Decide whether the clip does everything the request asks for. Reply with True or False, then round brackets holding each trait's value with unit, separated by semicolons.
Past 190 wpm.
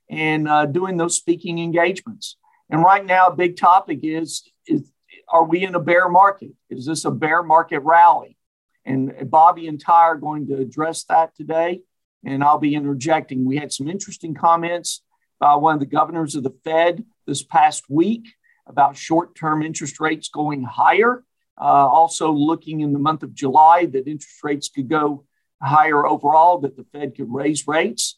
False (180 wpm)